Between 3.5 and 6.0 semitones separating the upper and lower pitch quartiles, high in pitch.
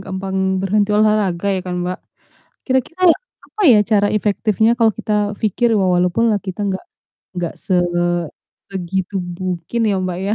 No: average, 2.7 semitones; high, 200 Hz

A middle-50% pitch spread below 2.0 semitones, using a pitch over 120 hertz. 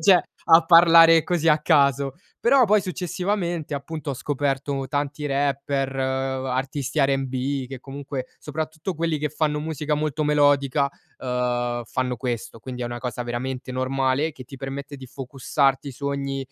No: narrow, 2.6 semitones; medium, 140 Hz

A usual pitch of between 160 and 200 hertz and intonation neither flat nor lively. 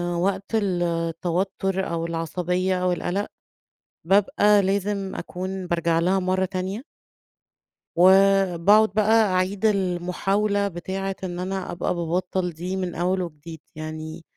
No: medium, 185 Hz; narrow, 2.0 semitones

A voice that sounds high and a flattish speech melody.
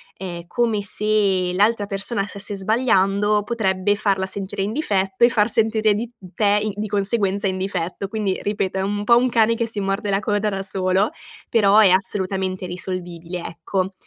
Yes: high, 200 Hz; narrow, 2.1 semitones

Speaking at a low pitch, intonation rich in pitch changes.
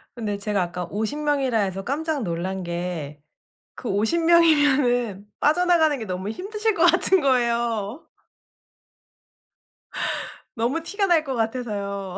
No: high, 235 Hz; wide, 7.7 semitones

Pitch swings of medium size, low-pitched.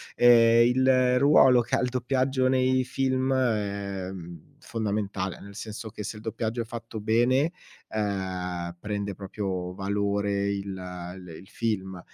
Yes: average, 4.2 semitones; low, 105 Hz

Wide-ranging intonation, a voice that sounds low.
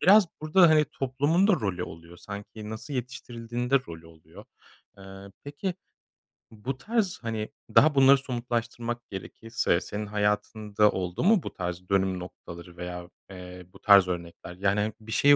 Yes: wide, 6.8 semitones; low, 110 Hz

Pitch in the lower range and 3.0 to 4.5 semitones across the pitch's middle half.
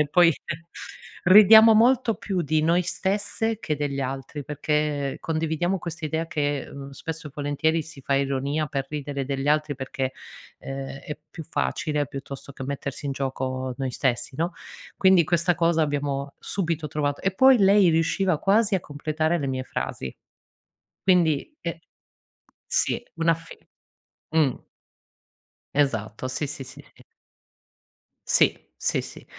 No: medium, 150 Hz; average, 3.6 semitones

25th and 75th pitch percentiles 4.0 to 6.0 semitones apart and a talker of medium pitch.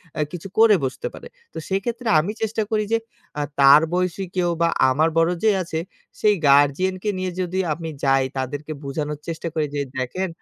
Yes: average, 4.7 semitones; medium, 165 Hz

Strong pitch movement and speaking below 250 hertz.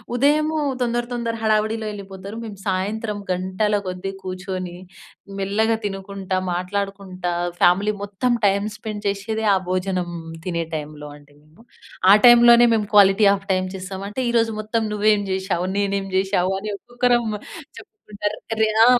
No: average, 2.8 semitones; high, 200 Hz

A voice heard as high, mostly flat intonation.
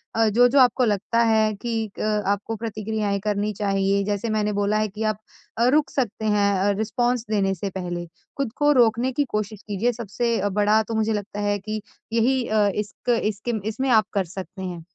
Yes: high, 215 Hz; narrow, 2.1 semitones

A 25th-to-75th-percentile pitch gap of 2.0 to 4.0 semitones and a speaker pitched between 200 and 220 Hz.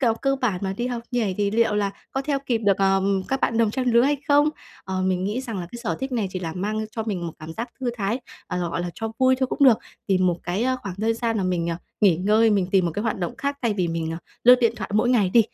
No: average, 4.5 semitones; high, 215 Hz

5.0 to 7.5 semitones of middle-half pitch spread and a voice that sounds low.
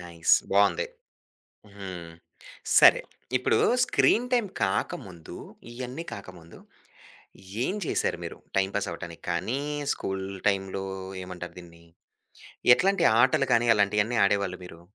Yes: wide, 5.5 semitones; very low, 95 Hz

